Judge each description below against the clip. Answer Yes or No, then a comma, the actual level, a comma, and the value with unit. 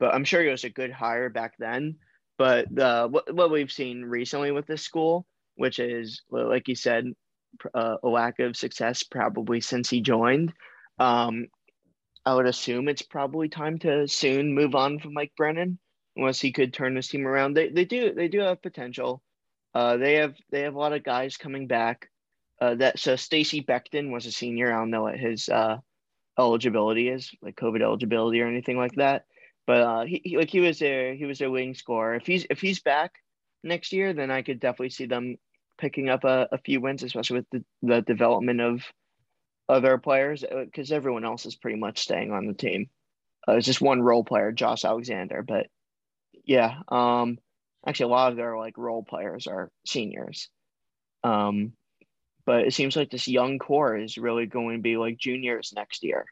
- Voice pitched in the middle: No, low, 130 Hz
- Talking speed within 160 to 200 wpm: Yes, average, 195 wpm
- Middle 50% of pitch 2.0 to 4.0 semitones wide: Yes, average, 3.3 semitones